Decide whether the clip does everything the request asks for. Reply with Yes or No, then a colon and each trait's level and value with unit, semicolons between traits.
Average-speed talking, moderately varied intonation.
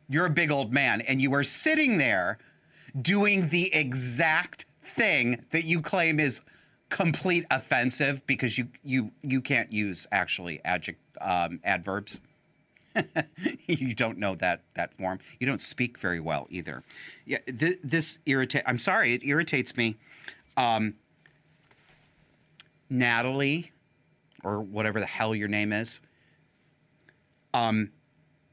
No: slow, 130 wpm; average, 4.4 semitones